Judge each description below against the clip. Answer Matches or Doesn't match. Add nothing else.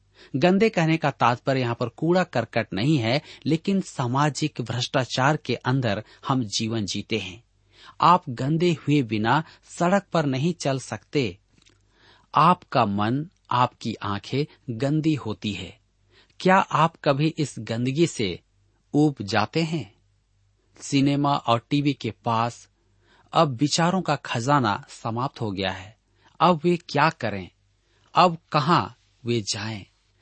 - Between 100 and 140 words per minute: Matches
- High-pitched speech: Doesn't match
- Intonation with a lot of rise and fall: Matches